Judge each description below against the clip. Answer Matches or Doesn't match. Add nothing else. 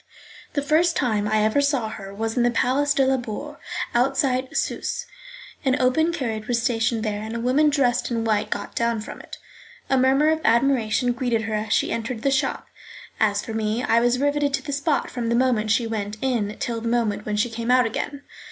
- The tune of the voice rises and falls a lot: Doesn't match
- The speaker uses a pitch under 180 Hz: Doesn't match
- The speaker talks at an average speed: Doesn't match